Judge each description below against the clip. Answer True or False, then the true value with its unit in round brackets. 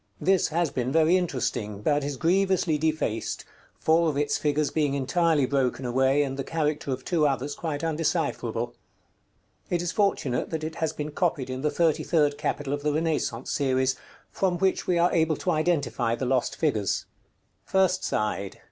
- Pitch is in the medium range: True (150 Hz)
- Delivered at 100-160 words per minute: False (175 wpm)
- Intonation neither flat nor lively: True (3.8 semitones)